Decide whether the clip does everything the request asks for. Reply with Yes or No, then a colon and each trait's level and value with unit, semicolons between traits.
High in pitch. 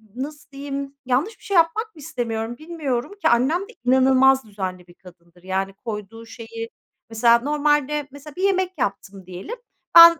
Yes: very high, 260 Hz